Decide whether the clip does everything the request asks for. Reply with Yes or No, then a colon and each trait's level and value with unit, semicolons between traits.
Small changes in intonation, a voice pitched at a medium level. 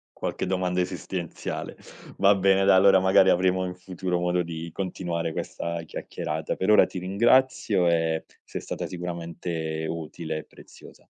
No: narrow, 2.1 semitones; very low, 90 Hz